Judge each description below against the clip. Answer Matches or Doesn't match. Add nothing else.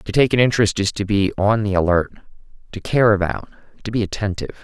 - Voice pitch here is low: Matches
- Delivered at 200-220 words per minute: Matches